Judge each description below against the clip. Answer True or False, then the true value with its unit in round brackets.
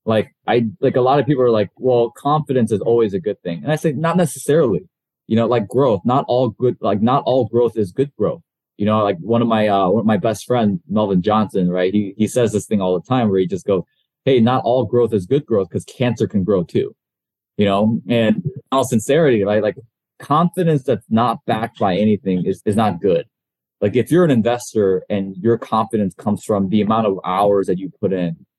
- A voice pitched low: True (110 Hz)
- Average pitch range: True (3.8 semitones)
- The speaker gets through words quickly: True (230 wpm)